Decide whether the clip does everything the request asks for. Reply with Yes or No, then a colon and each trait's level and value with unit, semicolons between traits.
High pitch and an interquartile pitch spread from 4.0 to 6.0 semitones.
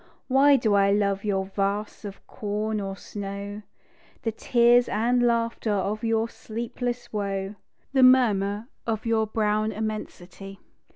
No: high, 215 Hz; narrow, 2.5 semitones